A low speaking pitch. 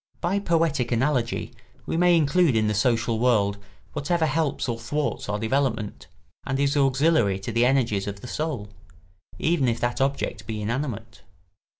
Yes: low, 125 Hz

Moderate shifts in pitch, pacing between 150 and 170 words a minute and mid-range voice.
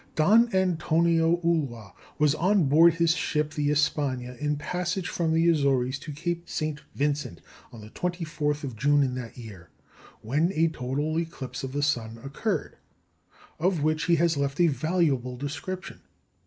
Yes: average, 3.6 semitones; average, 155 wpm; medium, 150 Hz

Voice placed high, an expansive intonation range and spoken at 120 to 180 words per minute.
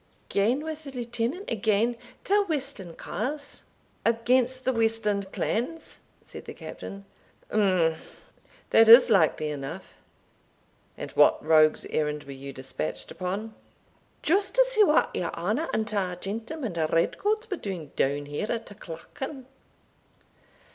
Yes: high, 220 Hz; wide, 7.1 semitones; slow, 135 wpm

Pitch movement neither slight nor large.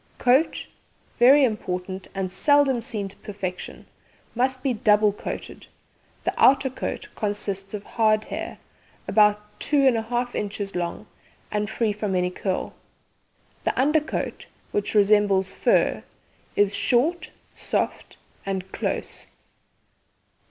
Yes: average, 4.1 semitones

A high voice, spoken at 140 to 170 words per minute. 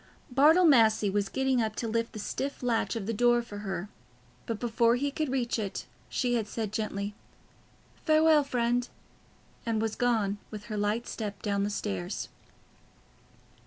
Yes: high, 230 Hz; average, 160 wpm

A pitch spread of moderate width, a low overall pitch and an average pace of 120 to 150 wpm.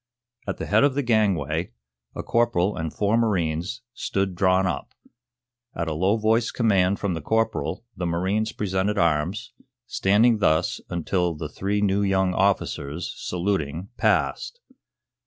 Yes: average, 3.9 semitones; very low, 95 Hz; average, 140 wpm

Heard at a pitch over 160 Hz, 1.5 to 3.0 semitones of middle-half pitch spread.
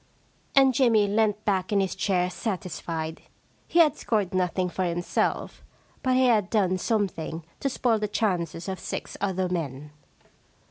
No: high, 190 Hz; average, 3.7 semitones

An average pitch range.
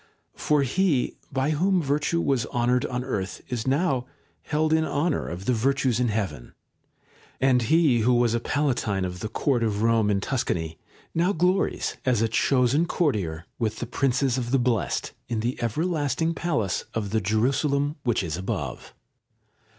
Yes: average, 4.7 semitones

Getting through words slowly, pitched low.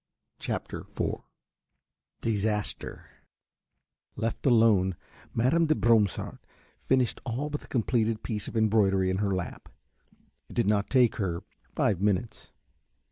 Yes: slow, 120 wpm; low, 110 Hz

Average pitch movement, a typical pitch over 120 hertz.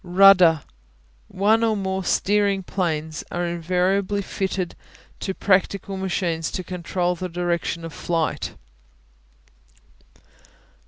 No: narrow, 2.2 semitones; medium, 185 Hz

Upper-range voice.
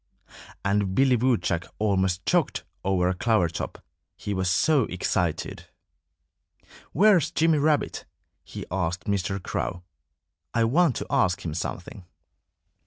No: low, 100 Hz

